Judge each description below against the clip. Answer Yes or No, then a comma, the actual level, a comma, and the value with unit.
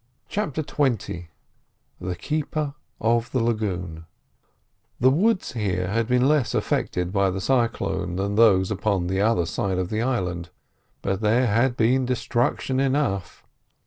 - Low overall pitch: Yes, low, 110 Hz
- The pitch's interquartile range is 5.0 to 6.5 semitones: Yes, wide, 5.6 semitones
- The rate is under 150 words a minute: Yes, average, 140 wpm